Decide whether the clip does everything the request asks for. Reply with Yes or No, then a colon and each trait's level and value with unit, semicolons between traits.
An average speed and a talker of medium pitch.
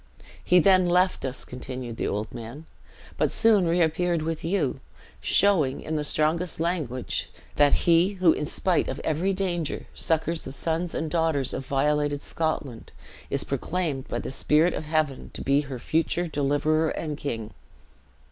Yes: average, 155 wpm; medium, 155 Hz